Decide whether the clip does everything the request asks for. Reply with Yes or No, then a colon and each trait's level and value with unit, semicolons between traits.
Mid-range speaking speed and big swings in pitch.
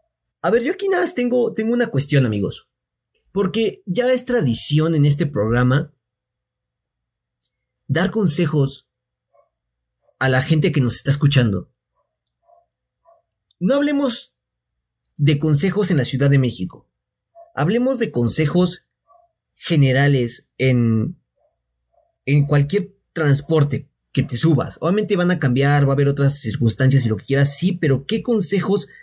Yes: average, 135 wpm; wide, 7.6 semitones